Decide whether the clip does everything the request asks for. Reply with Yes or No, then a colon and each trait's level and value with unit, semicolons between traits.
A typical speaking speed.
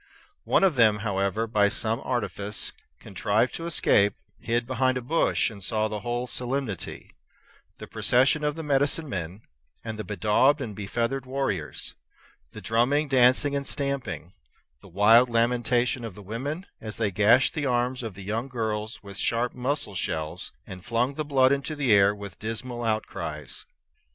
Yes: average, 160 wpm